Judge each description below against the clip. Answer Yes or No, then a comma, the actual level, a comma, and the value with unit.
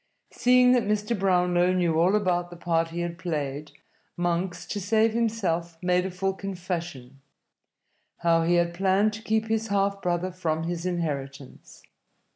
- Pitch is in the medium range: Yes, medium, 180 Hz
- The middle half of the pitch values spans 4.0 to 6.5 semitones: No, average, 2.8 semitones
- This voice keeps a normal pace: Yes, average, 155 wpm